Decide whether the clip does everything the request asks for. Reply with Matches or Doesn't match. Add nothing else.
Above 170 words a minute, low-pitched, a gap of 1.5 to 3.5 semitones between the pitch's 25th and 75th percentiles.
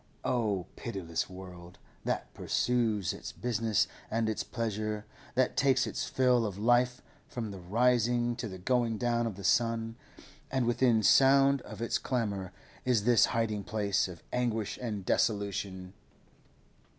Doesn't match